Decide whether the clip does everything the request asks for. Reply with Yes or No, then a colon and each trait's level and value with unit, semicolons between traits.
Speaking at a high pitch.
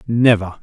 No: low, 110 Hz